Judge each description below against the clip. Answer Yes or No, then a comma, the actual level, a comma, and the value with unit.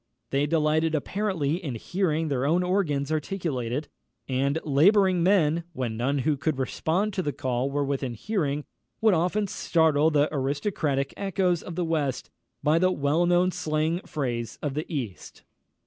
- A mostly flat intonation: No, average, 4.1 semitones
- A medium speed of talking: Yes, average, 160 wpm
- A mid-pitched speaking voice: Yes, medium, 155 Hz